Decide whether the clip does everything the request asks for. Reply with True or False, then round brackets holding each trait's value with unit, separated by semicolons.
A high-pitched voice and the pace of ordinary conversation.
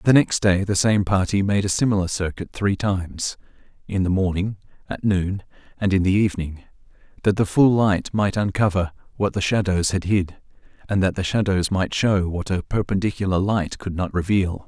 False (95 Hz; 175 wpm)